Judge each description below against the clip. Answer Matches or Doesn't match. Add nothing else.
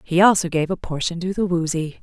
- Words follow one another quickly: Matches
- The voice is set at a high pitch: Doesn't match